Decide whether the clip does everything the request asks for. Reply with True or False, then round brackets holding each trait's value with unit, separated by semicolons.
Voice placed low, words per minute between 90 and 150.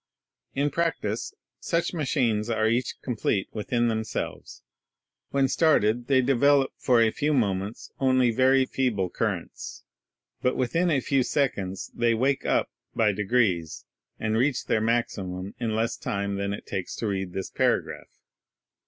True (115 Hz; 145 wpm)